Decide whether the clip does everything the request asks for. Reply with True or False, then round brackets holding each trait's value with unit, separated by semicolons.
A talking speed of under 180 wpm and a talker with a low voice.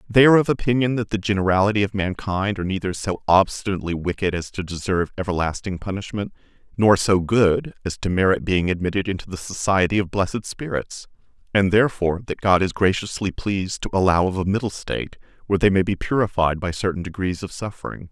False (185 wpm; 100 Hz)